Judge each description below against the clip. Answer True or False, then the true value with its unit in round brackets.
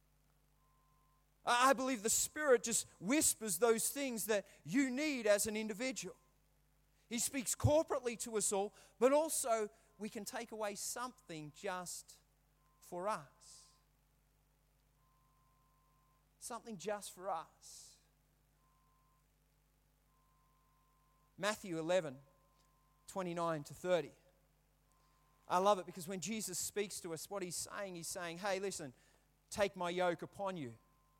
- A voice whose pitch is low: False (185 Hz)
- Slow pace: True (115 wpm)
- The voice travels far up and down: True (6.6 semitones)